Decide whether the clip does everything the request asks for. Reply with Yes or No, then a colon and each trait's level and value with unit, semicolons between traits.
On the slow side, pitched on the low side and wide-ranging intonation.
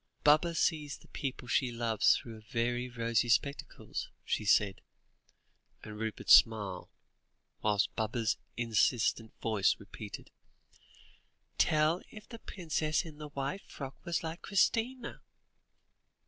Yes: slow, 115 wpm; low, 125 Hz; wide, 5.9 semitones